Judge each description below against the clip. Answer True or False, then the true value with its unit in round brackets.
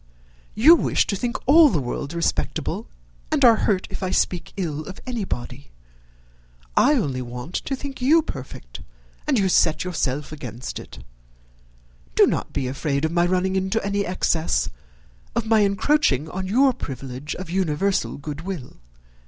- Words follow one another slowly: False (155 wpm)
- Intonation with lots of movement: True (7.2 semitones)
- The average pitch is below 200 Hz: True (185 Hz)